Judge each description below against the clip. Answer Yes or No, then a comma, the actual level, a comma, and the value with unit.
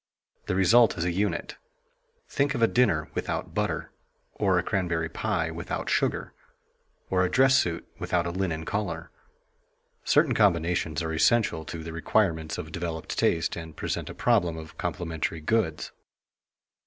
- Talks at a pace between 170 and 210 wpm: No, average, 150 wpm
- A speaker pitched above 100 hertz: No, very low, 85 Hz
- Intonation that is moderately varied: Yes, average, 3.1 semitones